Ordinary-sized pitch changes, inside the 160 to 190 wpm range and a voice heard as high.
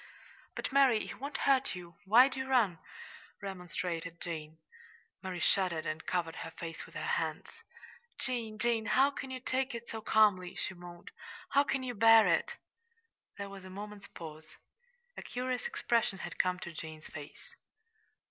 No: wide, 6.3 semitones; average, 165 wpm; high, 200 Hz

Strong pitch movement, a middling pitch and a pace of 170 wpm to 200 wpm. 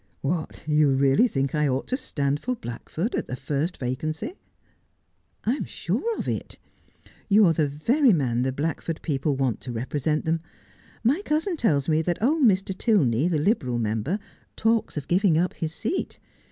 Yes: wide, 7.4 semitones; medium, 155 Hz; average, 180 wpm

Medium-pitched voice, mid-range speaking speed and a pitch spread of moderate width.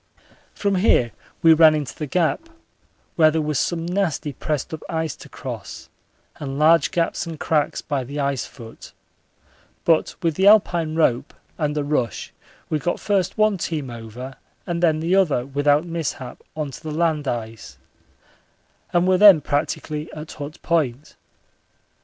Yes: medium, 155 Hz; average, 160 wpm; average, 3.1 semitones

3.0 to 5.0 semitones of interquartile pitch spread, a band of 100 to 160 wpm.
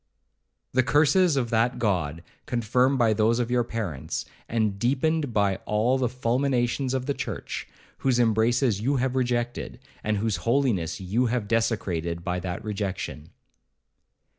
Yes: average, 3.7 semitones; average, 140 wpm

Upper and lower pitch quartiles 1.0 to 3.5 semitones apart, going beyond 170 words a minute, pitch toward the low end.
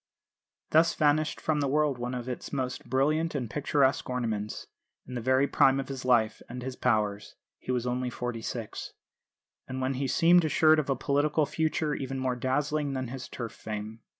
Yes: average, 3.1 semitones; average, 185 wpm; low, 130 Hz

